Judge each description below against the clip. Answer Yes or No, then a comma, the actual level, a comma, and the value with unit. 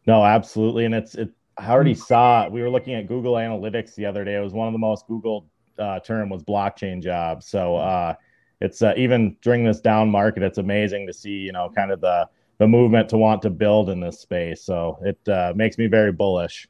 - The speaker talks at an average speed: No, fast, 225 wpm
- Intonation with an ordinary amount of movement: No, narrow, 2.1 semitones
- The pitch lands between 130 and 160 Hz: No, low, 110 Hz